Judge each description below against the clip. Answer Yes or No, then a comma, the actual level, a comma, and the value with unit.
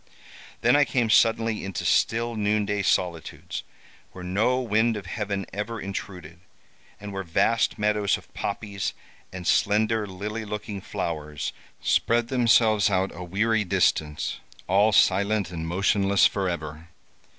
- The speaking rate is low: Yes, slow, 130 wpm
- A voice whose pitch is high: No, low, 100 Hz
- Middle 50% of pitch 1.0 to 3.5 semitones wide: Yes, average, 2.9 semitones